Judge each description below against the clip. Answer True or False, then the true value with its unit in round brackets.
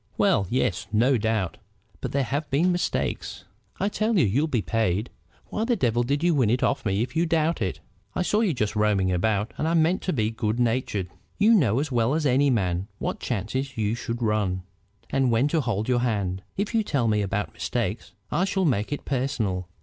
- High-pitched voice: False (120 Hz)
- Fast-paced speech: True (210 wpm)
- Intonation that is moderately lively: False (5.9 semitones)